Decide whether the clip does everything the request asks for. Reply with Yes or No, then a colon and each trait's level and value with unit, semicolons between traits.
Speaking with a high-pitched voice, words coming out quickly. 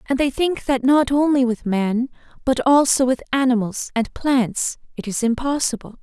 No: very high, 255 Hz; average, 170 wpm